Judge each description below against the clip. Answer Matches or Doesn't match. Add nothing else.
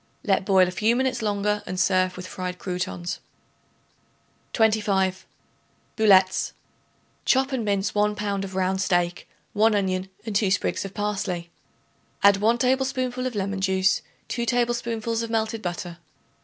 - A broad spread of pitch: Doesn't match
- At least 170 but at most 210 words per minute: Doesn't match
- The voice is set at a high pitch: Matches